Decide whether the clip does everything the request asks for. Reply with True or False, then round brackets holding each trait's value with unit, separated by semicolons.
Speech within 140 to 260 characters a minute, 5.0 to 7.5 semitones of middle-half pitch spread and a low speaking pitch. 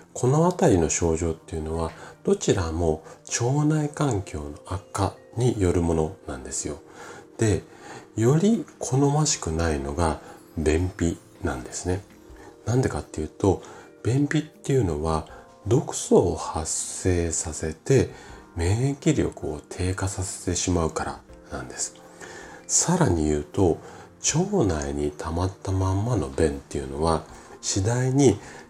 False (255 characters per minute; 8.0 semitones; 90 Hz)